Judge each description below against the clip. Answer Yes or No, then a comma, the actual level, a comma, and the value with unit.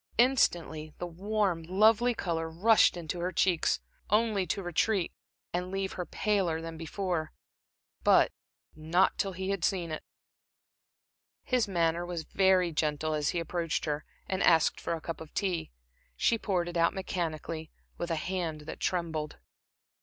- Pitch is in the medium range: Yes, medium, 175 Hz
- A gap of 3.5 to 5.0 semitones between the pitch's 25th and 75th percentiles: No, average, 2.9 semitones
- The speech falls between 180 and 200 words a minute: No, average, 155 wpm